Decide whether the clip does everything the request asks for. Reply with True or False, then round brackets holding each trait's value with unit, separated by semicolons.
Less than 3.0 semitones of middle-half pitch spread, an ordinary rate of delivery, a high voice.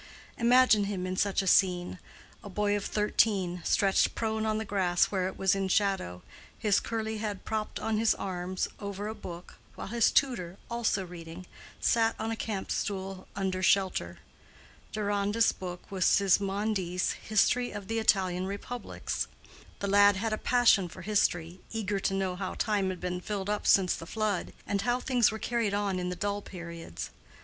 True (2.6 semitones; 175 wpm; 200 Hz)